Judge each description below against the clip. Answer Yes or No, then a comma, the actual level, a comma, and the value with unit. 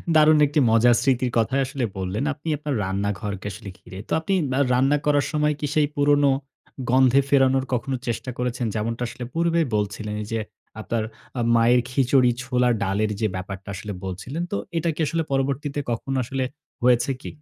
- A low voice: Yes, low, 125 Hz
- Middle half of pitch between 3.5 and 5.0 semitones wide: Yes, average, 4.2 semitones